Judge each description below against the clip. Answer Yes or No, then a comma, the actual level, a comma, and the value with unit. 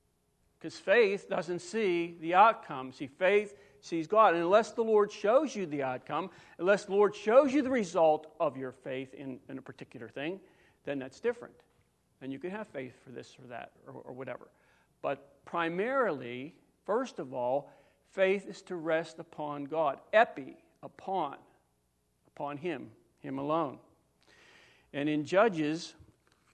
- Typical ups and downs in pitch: No, wide, 6.4 semitones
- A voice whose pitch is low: No, medium, 165 Hz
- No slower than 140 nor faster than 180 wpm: Yes, average, 155 wpm